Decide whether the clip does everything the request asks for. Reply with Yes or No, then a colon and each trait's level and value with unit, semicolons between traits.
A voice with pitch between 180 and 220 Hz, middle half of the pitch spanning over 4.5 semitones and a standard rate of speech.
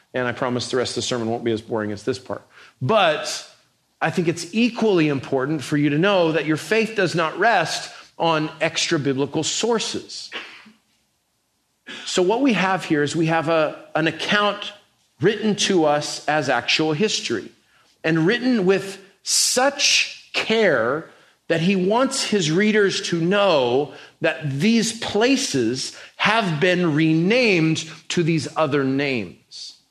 No: medium, 165 Hz; wide, 5.6 semitones; average, 150 wpm